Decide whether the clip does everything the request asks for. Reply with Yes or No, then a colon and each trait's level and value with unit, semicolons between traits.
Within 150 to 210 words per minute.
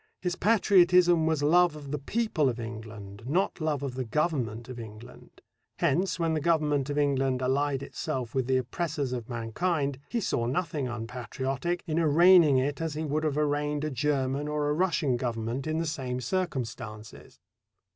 Yes: average, 170 wpm